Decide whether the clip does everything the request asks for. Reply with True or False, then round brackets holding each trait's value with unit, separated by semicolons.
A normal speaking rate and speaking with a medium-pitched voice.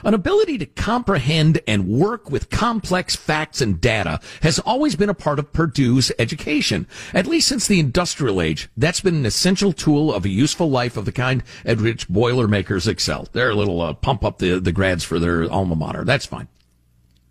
False (195 wpm; 125 Hz)